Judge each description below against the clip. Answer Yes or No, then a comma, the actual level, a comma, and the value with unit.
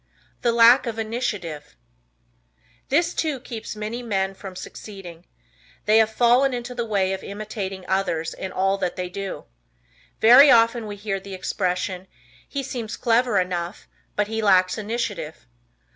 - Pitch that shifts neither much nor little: Yes, average, 3.8 semitones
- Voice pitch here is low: No, high, 210 Hz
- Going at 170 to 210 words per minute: No, average, 145 wpm